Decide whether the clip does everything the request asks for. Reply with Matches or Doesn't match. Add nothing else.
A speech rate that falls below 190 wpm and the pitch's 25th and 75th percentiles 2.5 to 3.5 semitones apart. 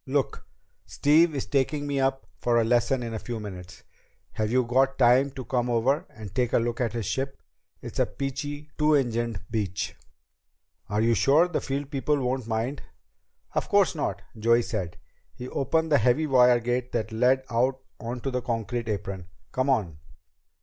Matches